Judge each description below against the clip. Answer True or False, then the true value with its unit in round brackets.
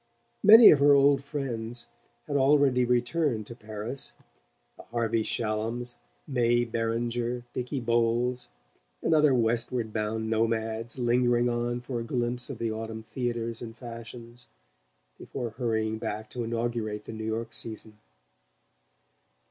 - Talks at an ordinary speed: False (130 wpm)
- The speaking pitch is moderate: False (120 Hz)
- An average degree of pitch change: False (1.6 semitones)